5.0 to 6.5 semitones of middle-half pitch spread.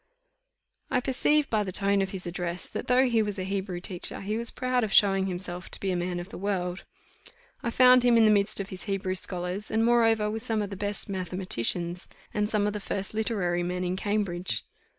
No: average, 3.1 semitones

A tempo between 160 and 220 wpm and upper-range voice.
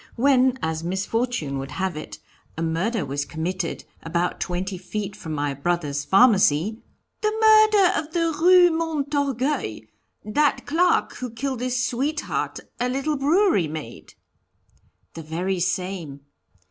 No: slow, 135 wpm; high, 215 Hz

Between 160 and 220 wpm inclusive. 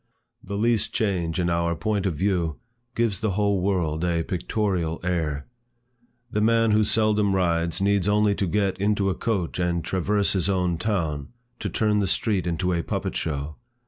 Yes: average, 175 wpm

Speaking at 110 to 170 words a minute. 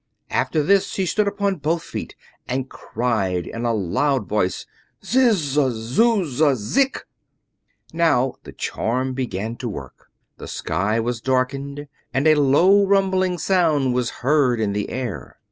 Yes: average, 145 wpm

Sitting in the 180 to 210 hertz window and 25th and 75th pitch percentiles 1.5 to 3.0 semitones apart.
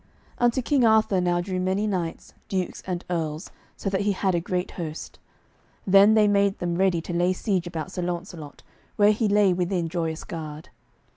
Yes: medium, 185 Hz; average, 2.7 semitones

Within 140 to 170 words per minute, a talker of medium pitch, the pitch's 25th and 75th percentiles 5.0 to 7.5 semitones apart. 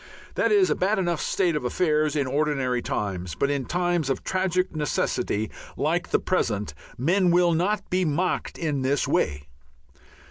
Yes: average, 165 wpm; medium, 155 Hz; average, 5.3 semitones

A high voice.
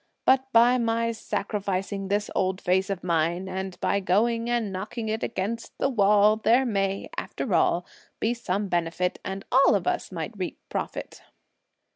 Yes: high, 200 Hz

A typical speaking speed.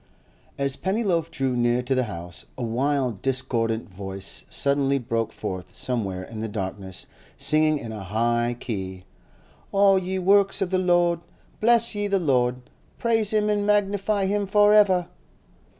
Yes: average, 150 wpm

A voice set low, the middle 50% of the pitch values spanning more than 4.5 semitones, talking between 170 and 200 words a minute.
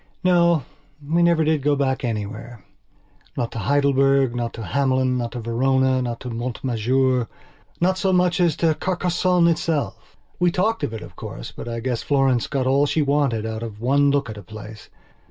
Yes: low, 130 Hz; average, 4.9 semitones; average, 185 wpm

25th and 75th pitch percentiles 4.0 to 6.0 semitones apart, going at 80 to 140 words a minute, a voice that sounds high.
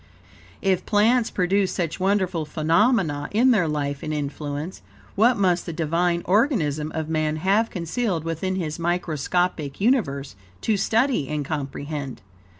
No: average, 4.6 semitones; slow, 135 wpm; medium, 170 Hz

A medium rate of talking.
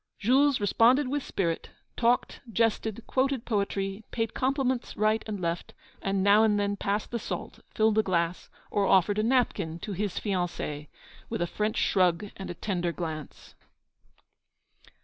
Yes: average, 150 wpm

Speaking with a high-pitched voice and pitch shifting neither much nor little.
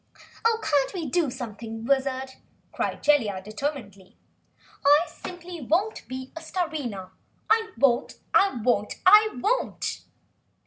No: very high, 275 Hz; wide, 6.8 semitones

